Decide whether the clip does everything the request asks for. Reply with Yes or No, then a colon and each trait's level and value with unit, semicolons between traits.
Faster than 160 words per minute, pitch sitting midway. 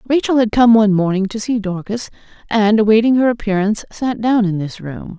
No: average, 195 wpm; high, 215 Hz